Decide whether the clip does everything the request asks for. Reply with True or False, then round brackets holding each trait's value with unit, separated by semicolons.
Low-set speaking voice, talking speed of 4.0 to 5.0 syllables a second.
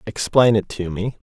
True (105 Hz; 4.7 syllables/s)